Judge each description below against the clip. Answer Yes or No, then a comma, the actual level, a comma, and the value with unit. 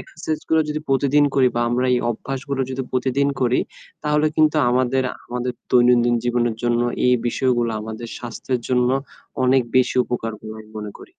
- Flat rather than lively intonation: Yes, narrow, 2.0 semitones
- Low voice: Yes, low, 125 Hz